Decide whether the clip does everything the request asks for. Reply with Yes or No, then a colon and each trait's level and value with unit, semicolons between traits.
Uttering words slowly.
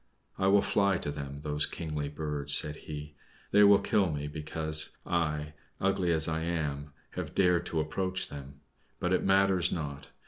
No: average, 170 wpm